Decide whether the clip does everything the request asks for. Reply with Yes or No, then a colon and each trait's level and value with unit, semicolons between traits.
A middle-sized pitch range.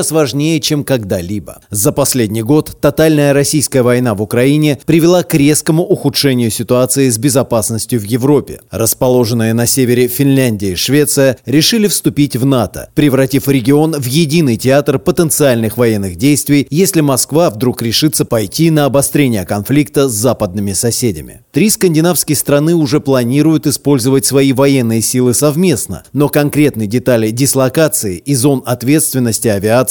Yes: average, 3.8 semitones